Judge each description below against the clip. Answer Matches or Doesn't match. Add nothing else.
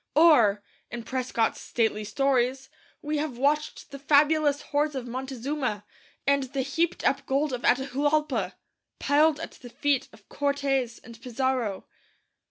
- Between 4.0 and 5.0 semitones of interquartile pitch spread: Doesn't match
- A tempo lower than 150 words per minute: Matches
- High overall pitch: Matches